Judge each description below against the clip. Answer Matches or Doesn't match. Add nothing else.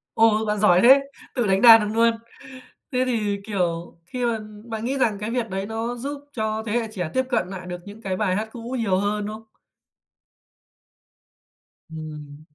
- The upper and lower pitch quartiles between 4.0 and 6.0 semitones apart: Doesn't match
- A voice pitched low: Doesn't match